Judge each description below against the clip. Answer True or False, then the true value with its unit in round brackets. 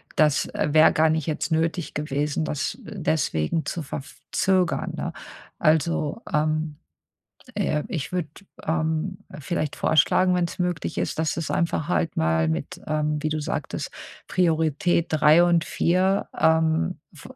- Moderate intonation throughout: False (2.3 semitones)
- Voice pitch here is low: False (160 Hz)